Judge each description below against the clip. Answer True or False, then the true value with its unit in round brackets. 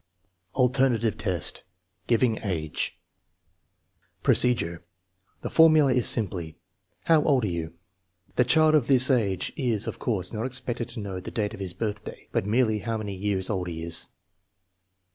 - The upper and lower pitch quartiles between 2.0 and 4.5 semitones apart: False (5.2 semitones)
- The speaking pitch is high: False (110 Hz)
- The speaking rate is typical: True (160 wpm)